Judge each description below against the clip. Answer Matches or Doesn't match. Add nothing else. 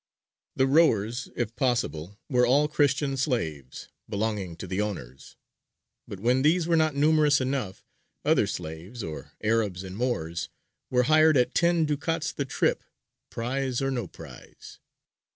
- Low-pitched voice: Matches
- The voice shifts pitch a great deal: Matches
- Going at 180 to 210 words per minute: Doesn't match